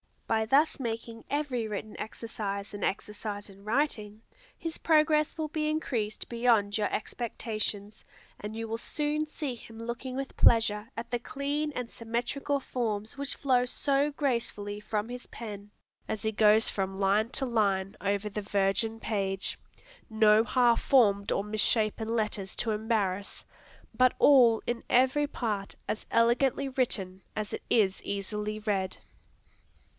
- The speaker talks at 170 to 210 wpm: No, average, 145 wpm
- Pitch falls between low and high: No, high, 225 Hz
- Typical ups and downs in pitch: Yes, average, 3.4 semitones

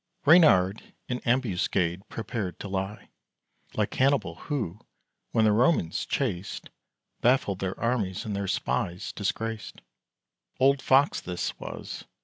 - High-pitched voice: No, low, 105 Hz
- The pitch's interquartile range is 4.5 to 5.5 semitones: Yes, average, 5.0 semitones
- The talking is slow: Yes, slow, 120 wpm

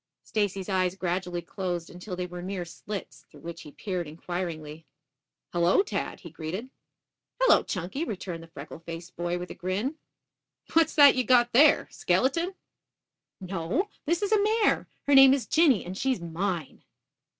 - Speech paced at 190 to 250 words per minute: No, average, 160 wpm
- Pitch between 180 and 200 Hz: Yes, medium, 185 Hz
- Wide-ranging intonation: Yes, wide, 7.1 semitones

